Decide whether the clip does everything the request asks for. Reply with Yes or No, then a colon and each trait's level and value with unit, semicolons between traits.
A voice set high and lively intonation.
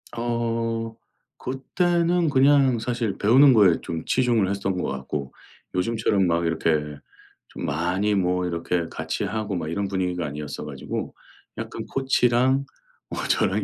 No: low, 100 Hz; wide, 5.9 semitones